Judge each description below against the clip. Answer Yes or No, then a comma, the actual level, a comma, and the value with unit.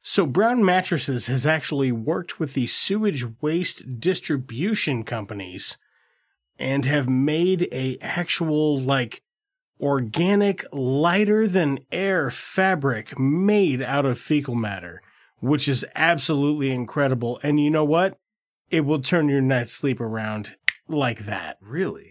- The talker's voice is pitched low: No, medium, 145 Hz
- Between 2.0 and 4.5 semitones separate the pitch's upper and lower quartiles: No, average, 5.0 semitones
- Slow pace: Yes, slow, 125 wpm